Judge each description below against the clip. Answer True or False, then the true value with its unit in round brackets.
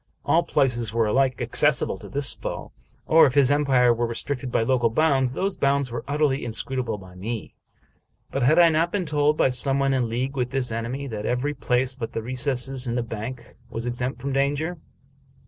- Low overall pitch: True (130 Hz)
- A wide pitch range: False (2.8 semitones)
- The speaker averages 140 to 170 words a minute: False (200 wpm)